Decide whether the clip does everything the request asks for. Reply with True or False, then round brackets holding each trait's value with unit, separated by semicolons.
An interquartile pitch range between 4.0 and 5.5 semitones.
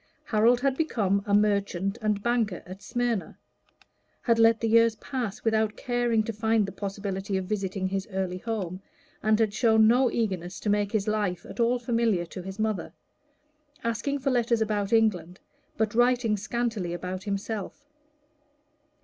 False (2.9 semitones)